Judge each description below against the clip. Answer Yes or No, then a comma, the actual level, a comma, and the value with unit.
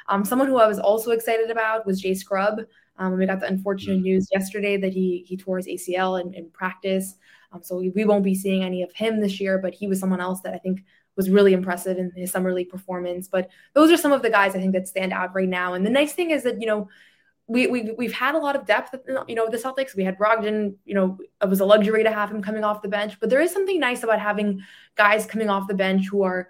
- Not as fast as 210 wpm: No, fast, 270 wpm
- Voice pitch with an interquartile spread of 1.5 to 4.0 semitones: Yes, average, 2.8 semitones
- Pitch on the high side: Yes, high, 200 Hz